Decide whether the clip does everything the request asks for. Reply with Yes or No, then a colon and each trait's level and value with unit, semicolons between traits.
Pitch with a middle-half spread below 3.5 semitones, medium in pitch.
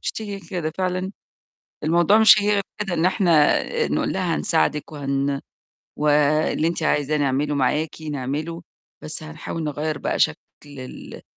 Yes: average, 3.0 semitones; medium, 155 Hz